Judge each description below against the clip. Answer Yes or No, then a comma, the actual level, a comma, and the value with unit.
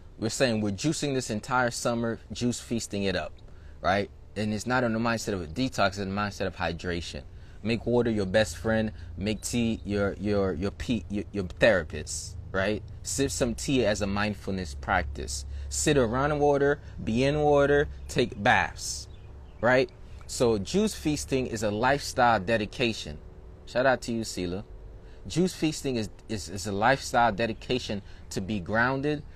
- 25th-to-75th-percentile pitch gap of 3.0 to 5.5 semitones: Yes, average, 4.7 semitones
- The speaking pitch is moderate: No, low, 105 Hz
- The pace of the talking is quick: No, average, 165 wpm